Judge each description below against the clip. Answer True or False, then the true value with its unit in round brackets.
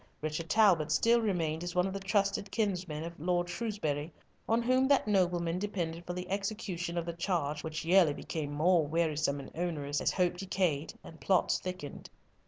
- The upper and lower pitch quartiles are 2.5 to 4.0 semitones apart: True (3.4 semitones)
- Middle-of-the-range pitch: True (175 Hz)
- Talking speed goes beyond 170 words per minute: True (180 wpm)